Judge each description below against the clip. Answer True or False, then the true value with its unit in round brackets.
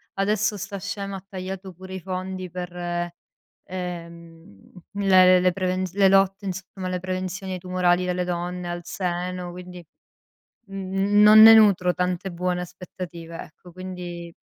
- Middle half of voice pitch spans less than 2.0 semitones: True (1.3 semitones)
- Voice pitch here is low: False (185 Hz)